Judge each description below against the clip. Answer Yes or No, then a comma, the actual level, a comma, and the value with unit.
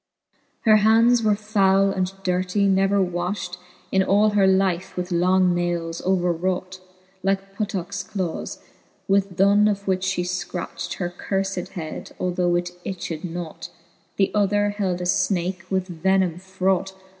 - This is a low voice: No, high, 190 Hz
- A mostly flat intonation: Yes, narrow, 1.8 semitones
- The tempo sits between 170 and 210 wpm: No, average, 145 wpm